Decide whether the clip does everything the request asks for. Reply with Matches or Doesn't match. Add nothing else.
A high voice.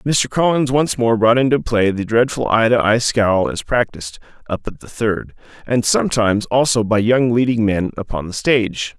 Doesn't match